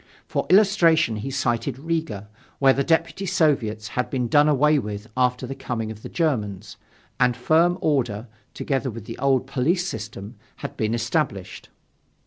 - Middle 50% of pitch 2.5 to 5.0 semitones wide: No, wide, 5.4 semitones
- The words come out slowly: No, average, 155 wpm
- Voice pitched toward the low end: Yes, low, 130 Hz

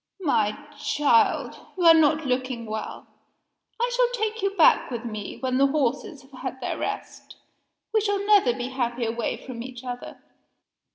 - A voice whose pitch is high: Yes, very high, 260 Hz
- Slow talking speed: No, average, 165 wpm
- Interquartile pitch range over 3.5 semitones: Yes, average, 5.2 semitones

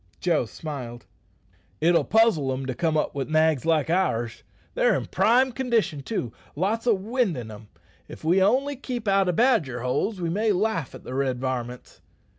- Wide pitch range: Yes, wide, 9.0 semitones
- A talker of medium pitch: Yes, medium, 165 Hz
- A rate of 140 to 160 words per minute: No, average, 180 wpm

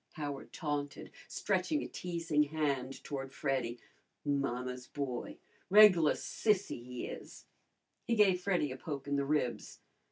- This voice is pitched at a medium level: Yes, medium, 145 Hz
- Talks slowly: Yes, slow, 130 wpm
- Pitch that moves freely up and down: No, average, 4.1 semitones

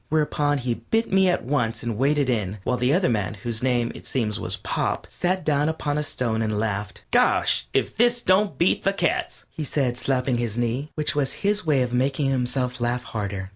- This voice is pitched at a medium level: No, low, 130 Hz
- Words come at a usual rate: No, fast, 210 wpm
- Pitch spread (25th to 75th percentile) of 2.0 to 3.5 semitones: No, average, 4.4 semitones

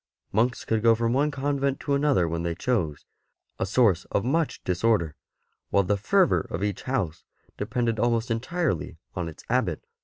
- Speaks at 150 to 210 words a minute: Yes, average, 180 wpm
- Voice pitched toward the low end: Yes, low, 115 Hz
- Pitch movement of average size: No, wide, 6.5 semitones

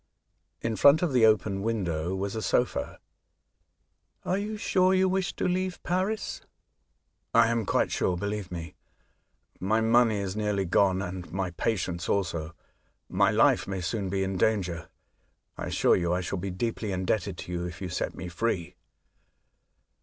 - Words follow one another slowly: No, average, 170 wpm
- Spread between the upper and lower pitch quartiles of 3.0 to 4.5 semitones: Yes, average, 4.2 semitones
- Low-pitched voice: Yes, low, 100 Hz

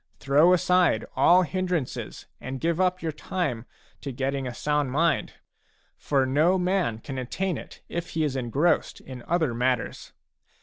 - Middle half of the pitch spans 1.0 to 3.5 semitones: No, average, 5.2 semitones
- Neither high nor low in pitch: Yes, medium, 150 Hz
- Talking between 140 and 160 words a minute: Yes, average, 150 wpm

